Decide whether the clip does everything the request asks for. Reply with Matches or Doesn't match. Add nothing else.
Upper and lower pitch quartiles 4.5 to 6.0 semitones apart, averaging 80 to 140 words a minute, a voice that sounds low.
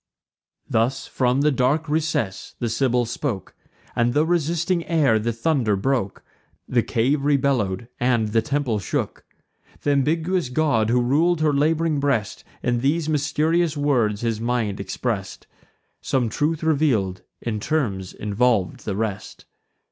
Matches